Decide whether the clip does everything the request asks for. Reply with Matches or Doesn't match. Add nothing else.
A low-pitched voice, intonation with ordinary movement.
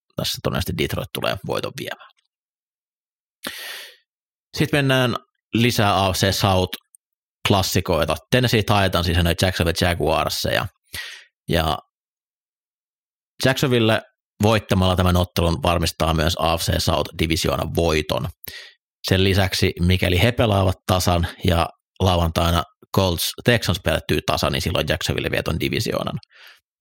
Matches